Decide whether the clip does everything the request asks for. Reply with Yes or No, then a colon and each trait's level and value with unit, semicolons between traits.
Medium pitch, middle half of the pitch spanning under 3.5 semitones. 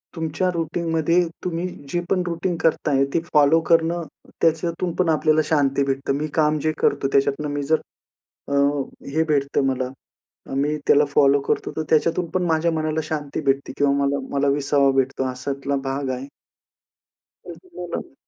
Yes: medium, 150 Hz; average, 2.8 semitones